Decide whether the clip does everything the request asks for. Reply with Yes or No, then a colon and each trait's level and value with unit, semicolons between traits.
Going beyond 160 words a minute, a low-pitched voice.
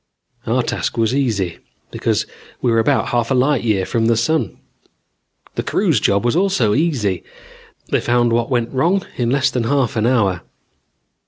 Yes: average, 170 wpm; low, 120 Hz